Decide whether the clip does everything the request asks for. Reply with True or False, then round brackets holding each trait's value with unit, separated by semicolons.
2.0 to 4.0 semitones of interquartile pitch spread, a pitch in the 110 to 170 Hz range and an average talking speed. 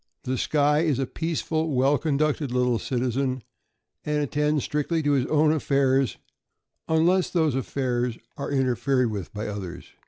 True (3.2 semitones; 140 Hz; 145 wpm)